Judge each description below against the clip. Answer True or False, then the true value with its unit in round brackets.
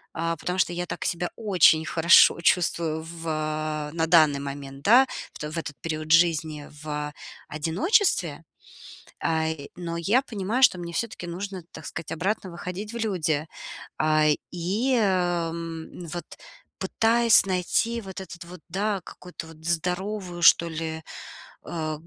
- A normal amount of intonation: True (3.1 semitones)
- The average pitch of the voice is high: False (170 Hz)